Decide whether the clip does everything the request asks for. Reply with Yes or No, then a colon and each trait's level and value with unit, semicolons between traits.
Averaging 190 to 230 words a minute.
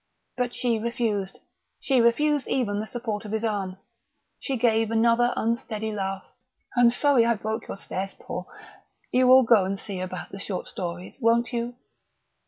No: average, 165 wpm